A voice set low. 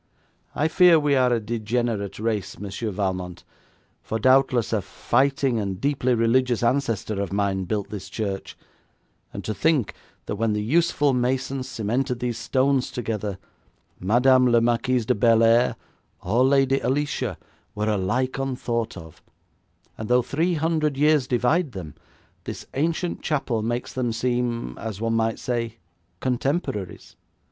Yes: low, 120 Hz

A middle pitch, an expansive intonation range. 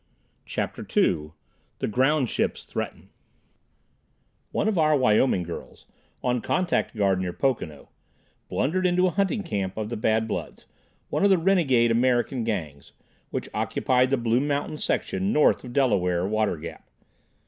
No: low, 125 Hz; wide, 6.9 semitones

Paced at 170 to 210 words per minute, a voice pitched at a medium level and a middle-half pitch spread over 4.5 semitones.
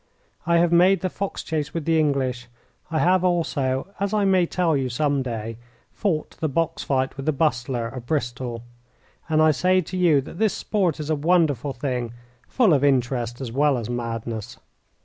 Yes: average, 190 wpm; medium, 145 Hz; average, 5.3 semitones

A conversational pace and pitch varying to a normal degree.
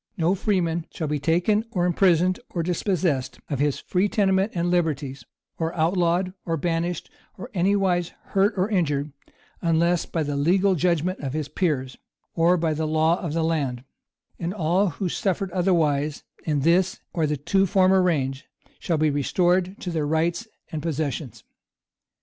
Yes: average, 160 wpm; average, 3.2 semitones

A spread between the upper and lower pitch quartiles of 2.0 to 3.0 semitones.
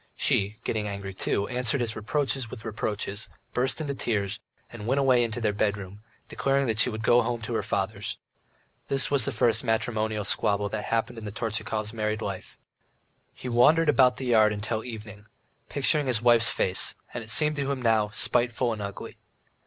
Yes: average, 2.7 semitones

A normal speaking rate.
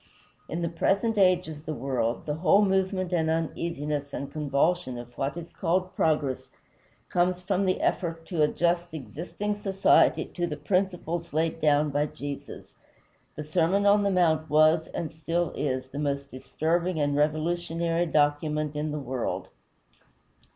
Yes: average, 150 wpm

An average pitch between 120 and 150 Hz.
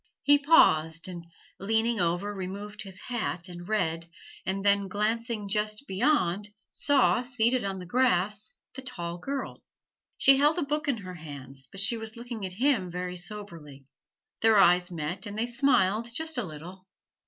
No: high, 205 Hz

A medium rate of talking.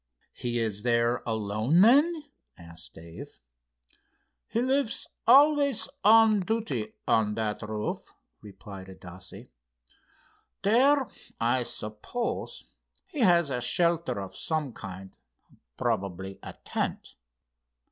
No: slow, 100 wpm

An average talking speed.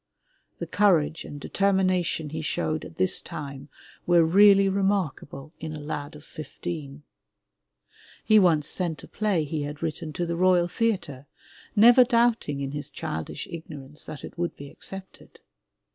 Yes: average, 150 wpm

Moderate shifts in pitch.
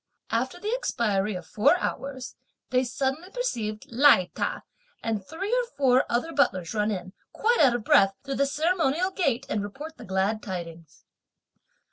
No: wide, 7.5 semitones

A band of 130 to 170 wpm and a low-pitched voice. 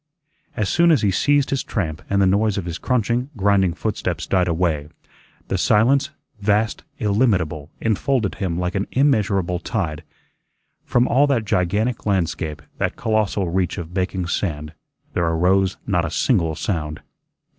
Yes: average, 150 wpm; very low, 95 Hz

